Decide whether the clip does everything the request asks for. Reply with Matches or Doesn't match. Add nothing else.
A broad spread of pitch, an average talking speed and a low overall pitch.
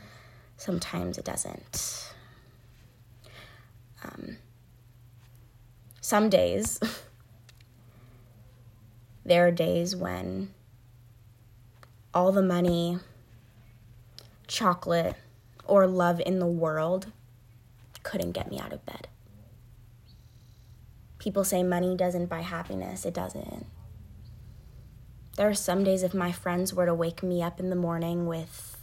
Doesn't match